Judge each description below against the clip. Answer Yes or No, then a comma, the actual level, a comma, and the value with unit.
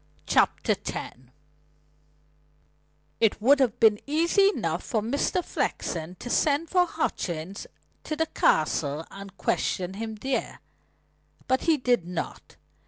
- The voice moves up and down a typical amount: No, wide, 7.9 semitones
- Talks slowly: Yes, slow, 120 wpm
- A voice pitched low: No, high, 230 Hz